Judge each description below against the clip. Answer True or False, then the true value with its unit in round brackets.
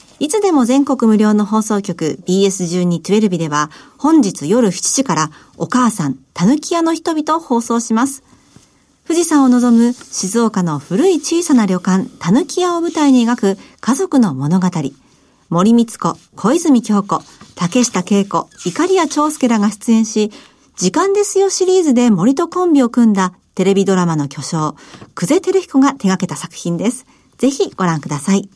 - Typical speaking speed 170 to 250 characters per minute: False (290 characters per minute)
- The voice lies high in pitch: True (225 Hz)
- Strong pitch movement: True (7.5 semitones)